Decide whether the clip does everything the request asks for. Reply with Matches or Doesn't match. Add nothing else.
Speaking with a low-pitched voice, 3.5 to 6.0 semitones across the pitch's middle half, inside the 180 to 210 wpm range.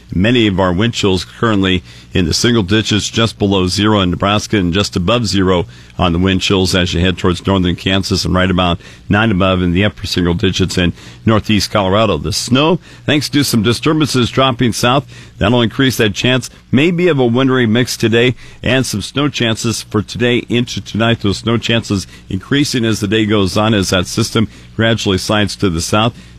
Matches